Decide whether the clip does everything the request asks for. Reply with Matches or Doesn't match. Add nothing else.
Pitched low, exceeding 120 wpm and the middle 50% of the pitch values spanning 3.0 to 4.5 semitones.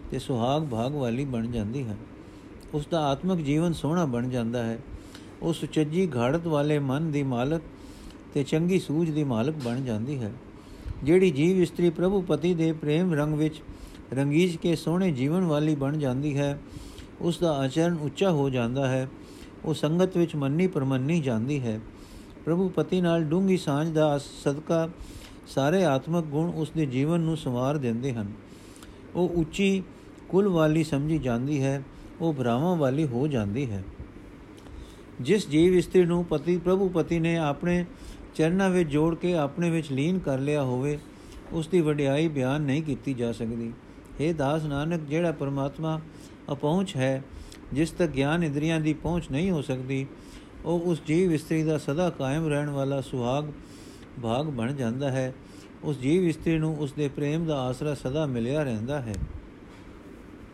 Doesn't match